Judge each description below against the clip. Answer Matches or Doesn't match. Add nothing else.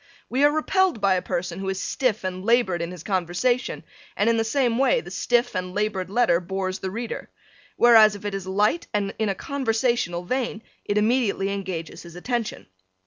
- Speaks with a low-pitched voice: Doesn't match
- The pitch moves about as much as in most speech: Matches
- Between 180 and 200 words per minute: Matches